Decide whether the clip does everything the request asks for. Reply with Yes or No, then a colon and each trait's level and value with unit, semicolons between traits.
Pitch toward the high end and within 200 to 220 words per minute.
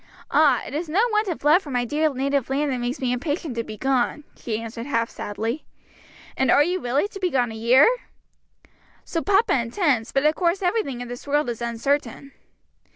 Yes: very high, 275 Hz; fast, 205 wpm